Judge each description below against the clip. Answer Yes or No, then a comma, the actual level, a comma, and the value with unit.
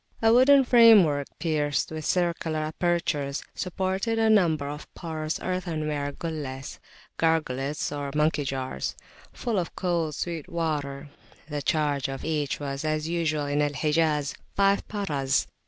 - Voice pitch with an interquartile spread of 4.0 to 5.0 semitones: No, average, 3.1 semitones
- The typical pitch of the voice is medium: Yes, medium, 155 Hz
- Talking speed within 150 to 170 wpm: No, slow, 135 wpm